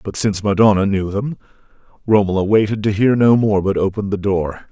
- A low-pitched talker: Yes, low, 100 Hz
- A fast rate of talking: No, average, 190 wpm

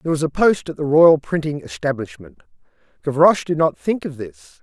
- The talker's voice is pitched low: No, medium, 150 Hz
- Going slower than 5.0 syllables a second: No, 5.6 syllables/s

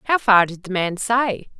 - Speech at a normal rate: No, fast, 225 wpm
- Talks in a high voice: Yes, high, 210 Hz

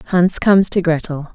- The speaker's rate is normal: Yes, average, 180 wpm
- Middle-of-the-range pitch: Yes, medium, 175 Hz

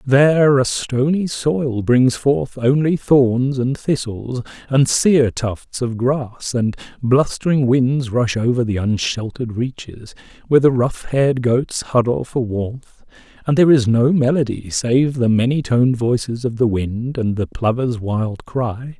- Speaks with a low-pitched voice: Yes, low, 125 Hz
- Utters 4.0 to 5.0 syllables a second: Yes, 4.1 syllables/s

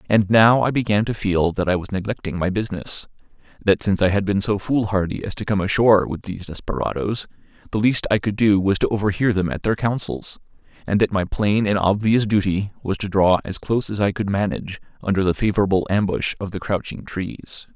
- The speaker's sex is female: No, male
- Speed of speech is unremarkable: No, fast, 210 wpm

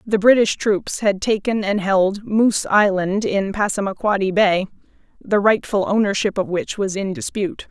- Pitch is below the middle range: No, high, 200 Hz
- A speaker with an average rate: Yes, average, 155 wpm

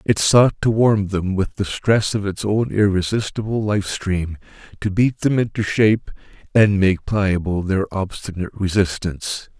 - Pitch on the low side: Yes, low, 100 Hz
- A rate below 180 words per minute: Yes, average, 155 wpm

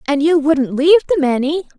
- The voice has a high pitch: Yes, very high, 305 Hz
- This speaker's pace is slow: No, average, 200 wpm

